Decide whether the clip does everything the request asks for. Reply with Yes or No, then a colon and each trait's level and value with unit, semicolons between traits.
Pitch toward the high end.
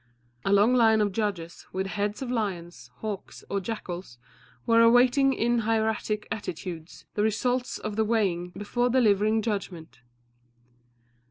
Yes: high, 210 Hz